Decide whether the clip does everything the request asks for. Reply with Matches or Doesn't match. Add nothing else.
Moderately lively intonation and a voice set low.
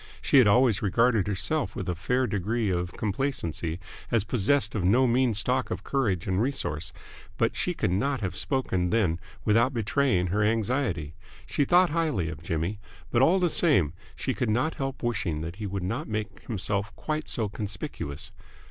Doesn't match